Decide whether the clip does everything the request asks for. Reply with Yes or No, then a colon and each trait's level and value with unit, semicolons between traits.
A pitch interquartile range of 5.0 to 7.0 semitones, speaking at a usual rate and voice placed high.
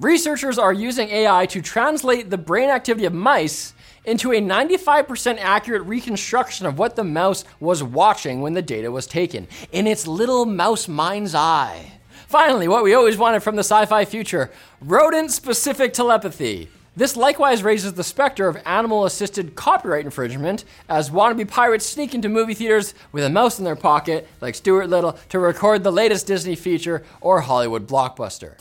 Yes: average, 5.3 semitones; average, 170 wpm; high, 205 Hz